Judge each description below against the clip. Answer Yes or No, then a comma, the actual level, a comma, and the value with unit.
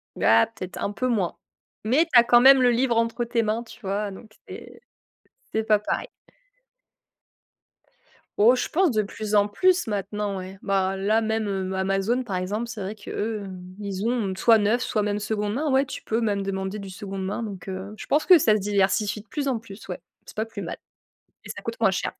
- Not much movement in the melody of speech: No, average, 3.0 semitones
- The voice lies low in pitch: No, high, 210 Hz